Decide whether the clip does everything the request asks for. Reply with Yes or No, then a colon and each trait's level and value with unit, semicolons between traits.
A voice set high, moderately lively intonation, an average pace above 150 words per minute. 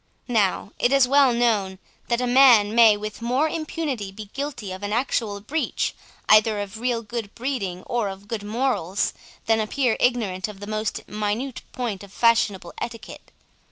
Yes: high, 225 Hz; average, 3.3 semitones; average, 165 wpm